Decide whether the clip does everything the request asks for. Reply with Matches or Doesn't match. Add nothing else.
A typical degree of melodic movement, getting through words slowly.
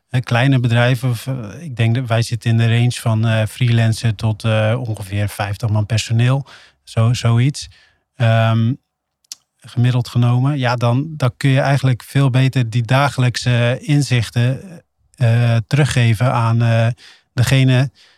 Doesn't match